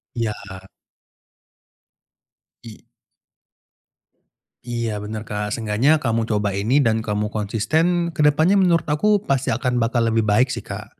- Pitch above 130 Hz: No, low, 115 Hz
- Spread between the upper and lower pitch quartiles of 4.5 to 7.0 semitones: Yes, wide, 5.5 semitones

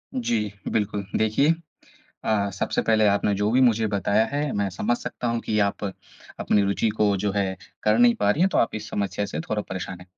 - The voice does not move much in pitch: Yes, narrow, 2.3 semitones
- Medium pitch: No, low, 105 Hz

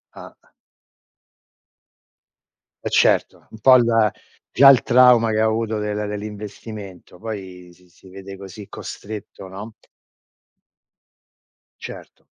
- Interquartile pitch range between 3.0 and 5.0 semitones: No, narrow, 2.5 semitones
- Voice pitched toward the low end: Yes, low, 105 Hz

